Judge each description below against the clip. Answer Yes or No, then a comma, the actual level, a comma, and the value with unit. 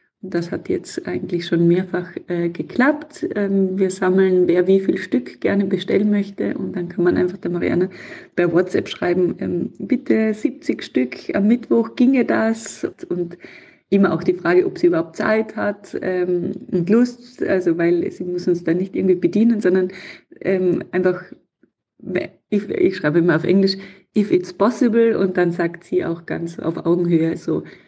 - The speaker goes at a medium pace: Yes, average, 170 wpm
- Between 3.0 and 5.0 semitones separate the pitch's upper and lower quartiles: Yes, average, 3.6 semitones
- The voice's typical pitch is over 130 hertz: Yes, medium, 185 Hz